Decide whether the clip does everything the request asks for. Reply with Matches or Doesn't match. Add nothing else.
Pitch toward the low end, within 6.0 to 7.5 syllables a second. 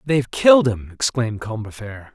Matches